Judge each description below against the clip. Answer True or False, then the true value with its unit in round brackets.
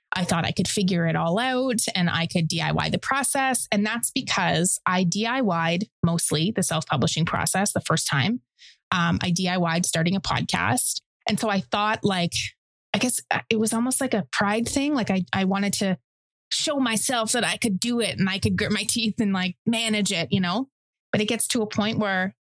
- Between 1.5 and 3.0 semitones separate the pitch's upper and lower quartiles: False (4.5 semitones)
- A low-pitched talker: False (200 Hz)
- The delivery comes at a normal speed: False (210 wpm)